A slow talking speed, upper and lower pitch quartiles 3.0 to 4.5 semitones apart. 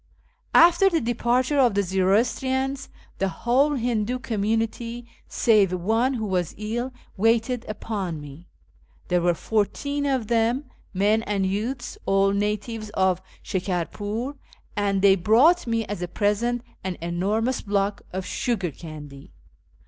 Yes: slow, 130 wpm; average, 4.0 semitones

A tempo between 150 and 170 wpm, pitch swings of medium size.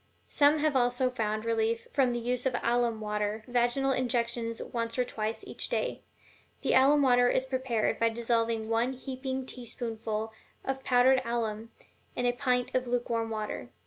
No: average, 160 wpm; narrow, 2.0 semitones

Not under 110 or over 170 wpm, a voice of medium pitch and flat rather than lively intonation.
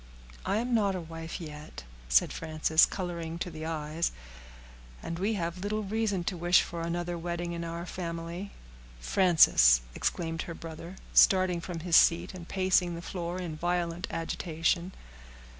Yes: average, 155 wpm; medium, 170 Hz; narrow, 1.8 semitones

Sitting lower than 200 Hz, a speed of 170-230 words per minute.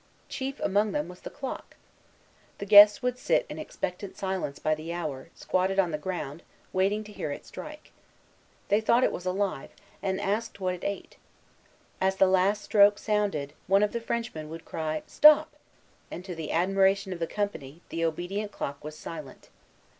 Yes: high, 190 Hz; average, 175 wpm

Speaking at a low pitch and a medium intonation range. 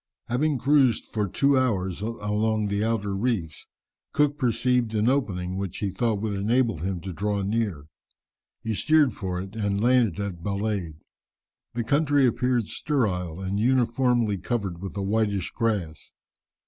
Yes: low, 110 Hz; average, 4.0 semitones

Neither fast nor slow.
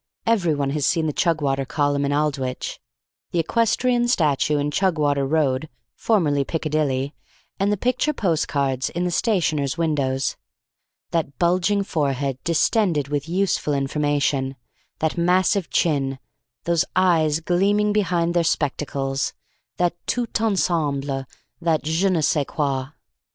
No: slow, 125 wpm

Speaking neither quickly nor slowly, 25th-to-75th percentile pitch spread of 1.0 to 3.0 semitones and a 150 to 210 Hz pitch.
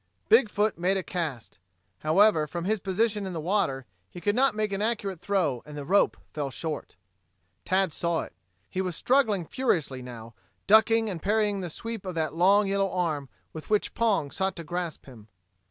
No: average, 185 wpm; average, 4.8 semitones; medium, 185 Hz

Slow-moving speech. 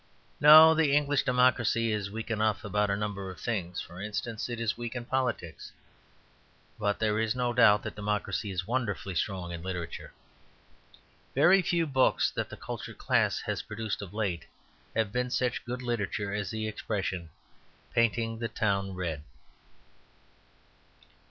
No: average, 150 wpm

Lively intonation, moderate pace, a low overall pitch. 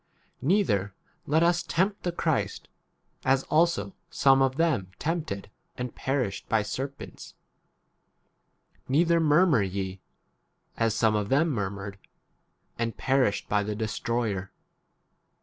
No: wide, 7.5 semitones; slow, 130 wpm; low, 125 Hz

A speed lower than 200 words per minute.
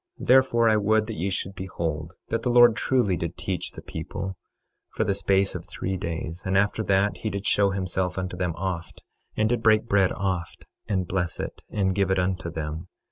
No: fast, 205 wpm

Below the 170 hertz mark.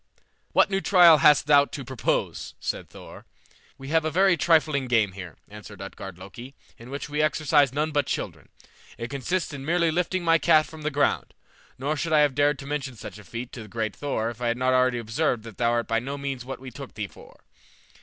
Yes: medium, 140 Hz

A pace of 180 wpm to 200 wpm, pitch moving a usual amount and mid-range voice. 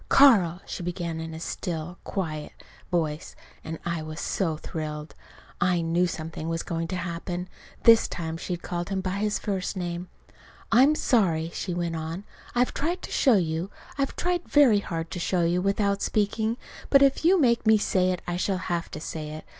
Yes: average, 185 wpm; average, 3.7 semitones; medium, 175 Hz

